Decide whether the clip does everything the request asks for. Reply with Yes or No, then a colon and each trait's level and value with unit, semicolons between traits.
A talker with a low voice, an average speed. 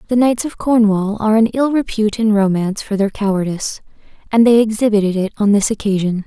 No: high, 210 Hz; average, 190 wpm